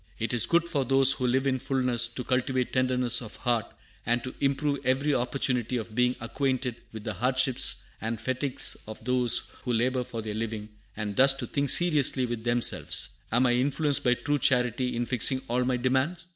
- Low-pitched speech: Yes, low, 125 Hz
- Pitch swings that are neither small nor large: No, narrow, 2.0 semitones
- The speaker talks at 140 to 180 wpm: No, average, 190 wpm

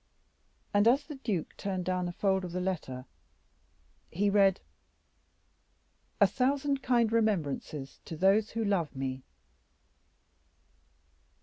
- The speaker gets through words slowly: Yes, slow, 115 wpm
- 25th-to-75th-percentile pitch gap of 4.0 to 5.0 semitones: Yes, average, 4.7 semitones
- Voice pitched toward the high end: Yes, high, 195 Hz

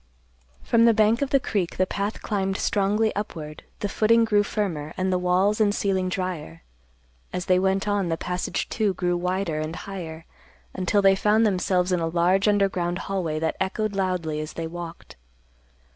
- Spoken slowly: No, average, 175 wpm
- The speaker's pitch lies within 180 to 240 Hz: Yes, high, 190 Hz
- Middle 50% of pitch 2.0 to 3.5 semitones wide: Yes, average, 2.9 semitones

